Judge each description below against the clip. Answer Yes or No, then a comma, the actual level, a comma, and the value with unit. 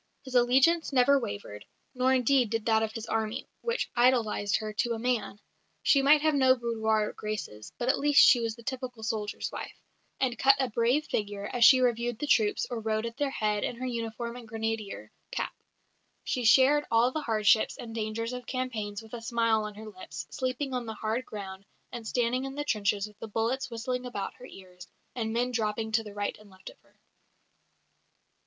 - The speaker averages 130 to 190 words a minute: No, average, 200 wpm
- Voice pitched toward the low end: No, high, 230 Hz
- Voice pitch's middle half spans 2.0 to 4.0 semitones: Yes, average, 2.8 semitones